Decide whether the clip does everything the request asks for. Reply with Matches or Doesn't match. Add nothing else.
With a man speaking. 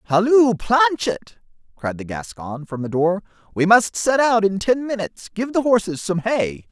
Matches